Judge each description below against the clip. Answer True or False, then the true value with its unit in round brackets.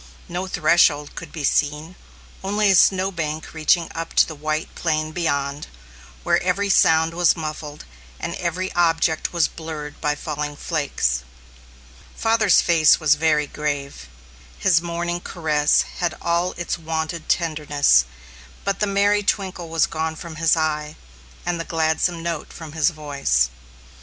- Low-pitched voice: False (160 Hz)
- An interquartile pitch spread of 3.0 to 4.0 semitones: False (2.4 semitones)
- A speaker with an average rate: True (145 wpm)